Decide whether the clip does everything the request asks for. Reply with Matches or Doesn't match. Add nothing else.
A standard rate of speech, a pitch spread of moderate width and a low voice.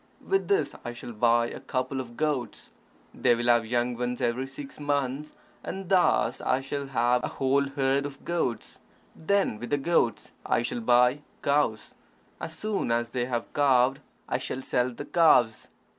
Matches